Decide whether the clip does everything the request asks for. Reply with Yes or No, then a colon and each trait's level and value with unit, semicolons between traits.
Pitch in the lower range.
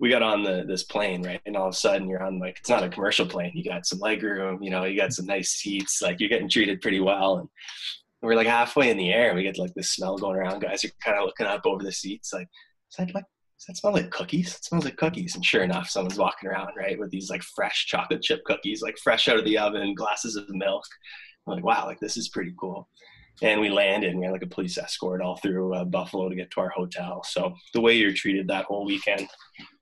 Yes: low, 100 Hz